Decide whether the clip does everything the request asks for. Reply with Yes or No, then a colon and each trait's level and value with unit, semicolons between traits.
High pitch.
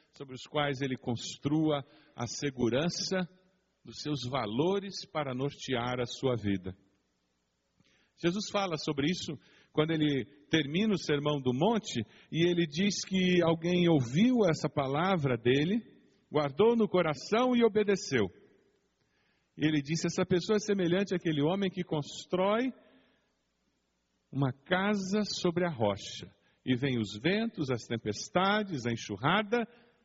No: medium, 155 Hz